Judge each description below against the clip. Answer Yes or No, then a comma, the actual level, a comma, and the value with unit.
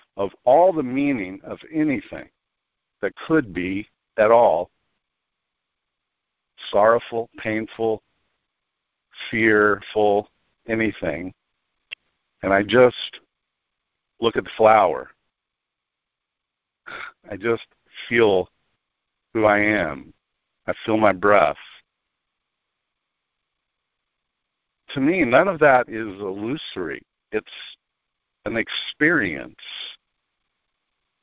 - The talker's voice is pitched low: Yes, low, 110 Hz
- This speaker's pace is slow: Yes, slow, 80 wpm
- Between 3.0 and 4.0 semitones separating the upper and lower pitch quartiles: Yes, average, 3.3 semitones